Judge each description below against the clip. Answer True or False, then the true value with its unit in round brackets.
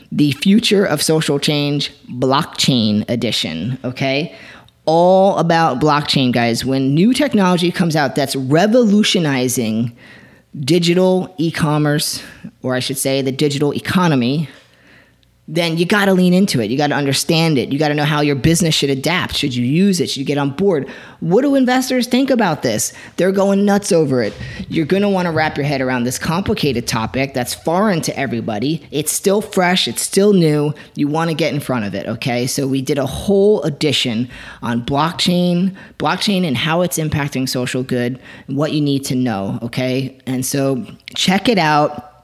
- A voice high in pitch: False (150 Hz)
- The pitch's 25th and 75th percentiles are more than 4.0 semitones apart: True (5.2 semitones)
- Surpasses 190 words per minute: False (180 wpm)